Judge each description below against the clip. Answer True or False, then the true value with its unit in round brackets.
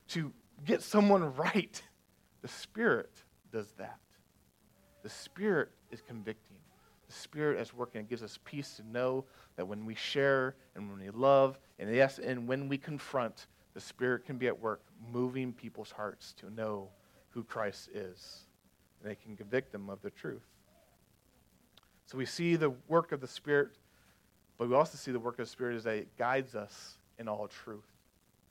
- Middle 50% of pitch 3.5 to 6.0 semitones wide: True (4.3 semitones)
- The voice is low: True (125 Hz)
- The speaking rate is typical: True (175 wpm)